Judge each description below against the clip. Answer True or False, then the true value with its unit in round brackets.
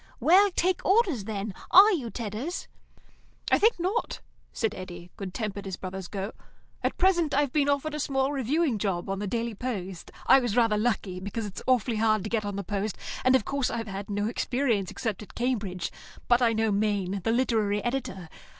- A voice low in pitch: False (225 Hz)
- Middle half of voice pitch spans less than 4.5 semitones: False (5.0 semitones)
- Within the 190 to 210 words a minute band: True (195 wpm)